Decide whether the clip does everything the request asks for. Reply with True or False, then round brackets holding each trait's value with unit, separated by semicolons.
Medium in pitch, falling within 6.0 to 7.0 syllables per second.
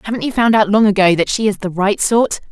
False (210 Hz; 6.1 syllables/s)